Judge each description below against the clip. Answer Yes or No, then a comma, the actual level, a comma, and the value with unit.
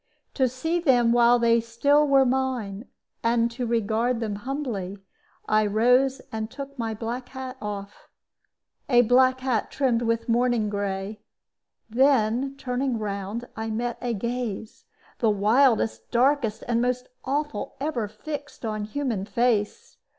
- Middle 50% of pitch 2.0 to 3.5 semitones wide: Yes, average, 3.1 semitones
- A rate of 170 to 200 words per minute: No, slow, 135 wpm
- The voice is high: Yes, high, 235 Hz